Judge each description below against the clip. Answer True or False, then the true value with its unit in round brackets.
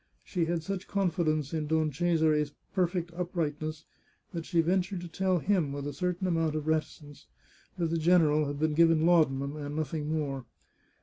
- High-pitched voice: False (160 Hz)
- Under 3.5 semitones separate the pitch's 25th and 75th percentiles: True (2.6 semitones)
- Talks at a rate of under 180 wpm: True (170 wpm)